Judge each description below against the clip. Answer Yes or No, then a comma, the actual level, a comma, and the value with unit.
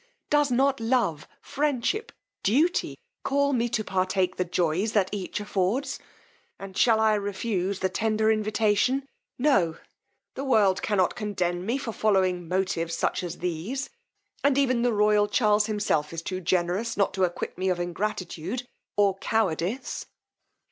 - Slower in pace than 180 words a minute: Yes, average, 145 wpm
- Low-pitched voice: No, high, 205 Hz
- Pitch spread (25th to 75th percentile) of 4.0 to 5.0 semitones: Yes, average, 4.3 semitones